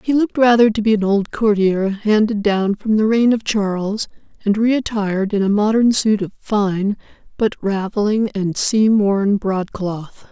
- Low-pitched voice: No, high, 210 Hz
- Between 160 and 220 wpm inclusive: Yes, average, 175 wpm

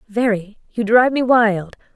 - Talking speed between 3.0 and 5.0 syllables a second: Yes, 4.5 syllables/s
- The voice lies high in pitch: Yes, high, 220 Hz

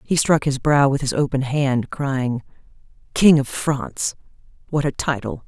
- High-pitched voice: No, low, 135 Hz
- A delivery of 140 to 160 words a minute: Yes, average, 155 wpm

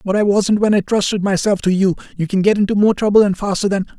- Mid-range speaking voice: No, high, 200 Hz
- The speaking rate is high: Yes, fast, 270 wpm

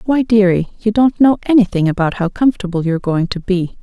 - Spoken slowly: No, fast, 205 wpm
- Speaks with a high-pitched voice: Yes, high, 200 Hz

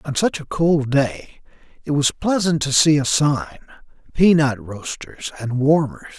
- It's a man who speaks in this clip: Yes, male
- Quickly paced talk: No, average, 155 wpm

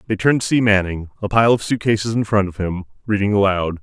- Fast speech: Yes, fast, 235 wpm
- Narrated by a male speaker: Yes, male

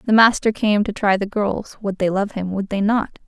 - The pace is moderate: No, fast, 255 wpm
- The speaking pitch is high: Yes, high, 205 Hz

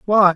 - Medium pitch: No, high, 195 Hz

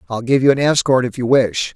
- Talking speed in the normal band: No, fast, 275 wpm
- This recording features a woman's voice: No, male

